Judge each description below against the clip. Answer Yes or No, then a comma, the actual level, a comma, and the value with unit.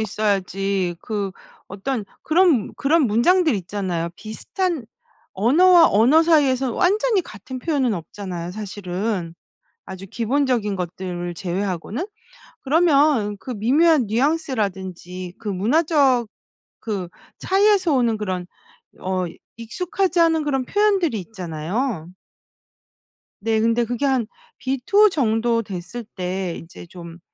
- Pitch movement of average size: No, wide, 7.5 semitones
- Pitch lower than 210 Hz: No, high, 225 Hz